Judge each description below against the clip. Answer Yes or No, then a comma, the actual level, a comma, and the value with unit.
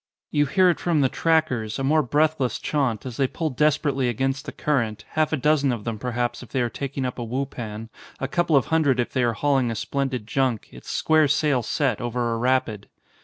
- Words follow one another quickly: Yes, fast, 220 wpm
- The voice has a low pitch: Yes, low, 130 Hz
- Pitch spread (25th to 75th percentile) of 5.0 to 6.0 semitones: No, average, 3.5 semitones